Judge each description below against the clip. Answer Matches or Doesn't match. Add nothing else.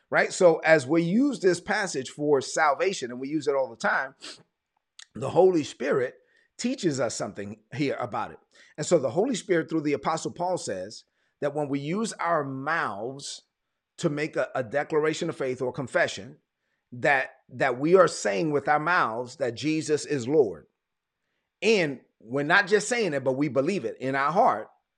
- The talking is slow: Doesn't match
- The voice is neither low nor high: Matches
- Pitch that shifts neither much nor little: Matches